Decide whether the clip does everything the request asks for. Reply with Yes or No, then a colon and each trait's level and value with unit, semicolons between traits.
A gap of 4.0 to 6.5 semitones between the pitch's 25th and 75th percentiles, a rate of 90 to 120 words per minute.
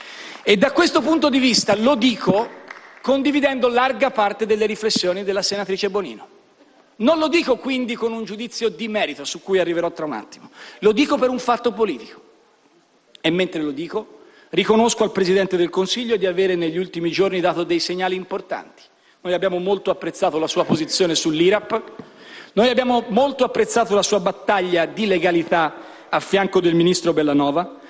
No: wide, 5.5 semitones; average, 165 wpm